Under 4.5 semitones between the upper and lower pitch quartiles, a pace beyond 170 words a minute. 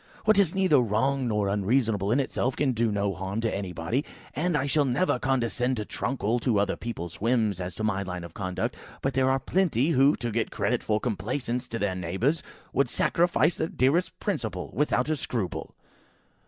No: average, 5.1 semitones; average, 190 wpm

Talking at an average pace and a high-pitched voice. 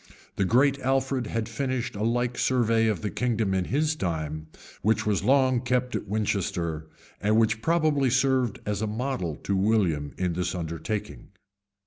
No: average, 160 wpm; low, 110 Hz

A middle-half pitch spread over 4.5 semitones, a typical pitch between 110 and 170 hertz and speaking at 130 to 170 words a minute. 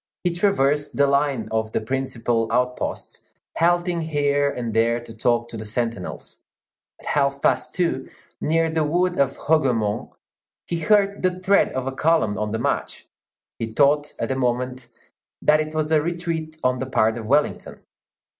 Yes: average, 5.2 semitones; medium, 140 Hz; average, 165 wpm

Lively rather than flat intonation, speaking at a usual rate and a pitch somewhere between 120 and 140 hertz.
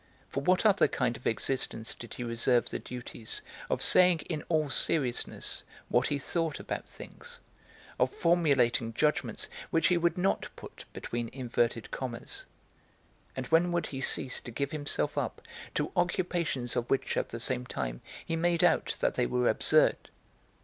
Yes: wide, 5.7 semitones; average, 165 wpm; low, 135 Hz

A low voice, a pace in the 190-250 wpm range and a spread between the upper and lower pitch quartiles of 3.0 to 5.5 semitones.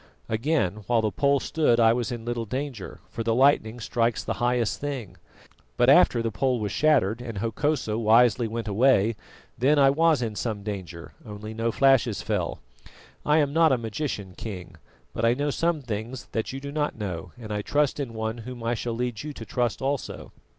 Yes: low, 120 Hz; average, 195 wpm; average, 3.8 semitones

